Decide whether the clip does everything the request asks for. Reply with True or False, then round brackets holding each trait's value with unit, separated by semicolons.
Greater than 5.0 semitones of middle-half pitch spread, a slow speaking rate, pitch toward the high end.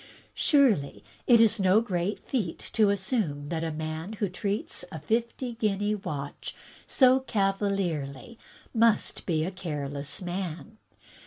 True (5.6 semitones; 130 wpm; 195 Hz)